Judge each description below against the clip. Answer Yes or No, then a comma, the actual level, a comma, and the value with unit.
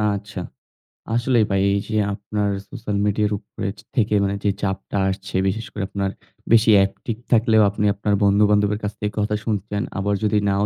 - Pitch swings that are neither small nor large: No, narrow, 1.2 semitones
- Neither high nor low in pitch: No, low, 105 Hz